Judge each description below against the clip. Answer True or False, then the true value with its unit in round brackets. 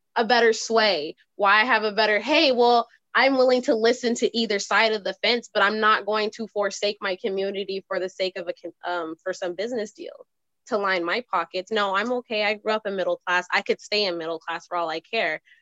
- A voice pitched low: False (210 Hz)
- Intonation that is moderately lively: True (3.4 semitones)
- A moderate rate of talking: False (235 wpm)